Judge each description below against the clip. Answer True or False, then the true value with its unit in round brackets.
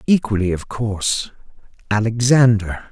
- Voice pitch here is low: True (110 Hz)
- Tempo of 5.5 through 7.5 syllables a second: False (4.6 syllables/s)